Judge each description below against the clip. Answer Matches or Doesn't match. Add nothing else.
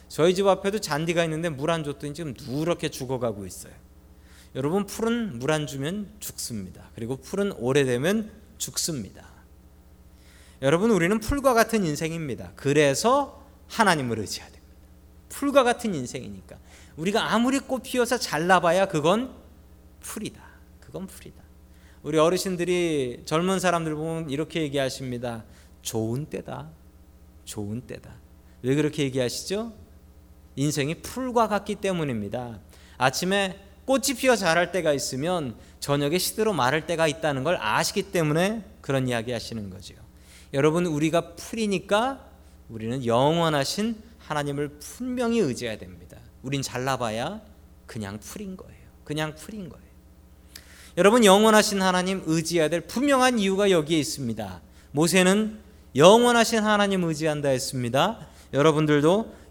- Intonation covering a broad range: Matches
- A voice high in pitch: Doesn't match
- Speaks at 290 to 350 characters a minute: Matches